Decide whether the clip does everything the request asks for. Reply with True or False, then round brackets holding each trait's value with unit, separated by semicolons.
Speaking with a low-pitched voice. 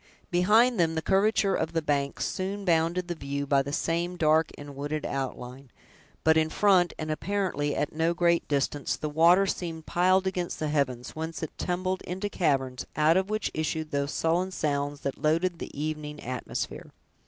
False (160 Hz)